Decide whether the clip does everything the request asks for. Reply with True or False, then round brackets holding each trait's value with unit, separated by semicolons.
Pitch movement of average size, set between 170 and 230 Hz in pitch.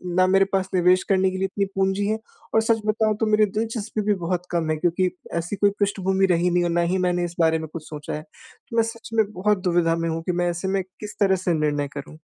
True (3.1 semitones; 185 Hz)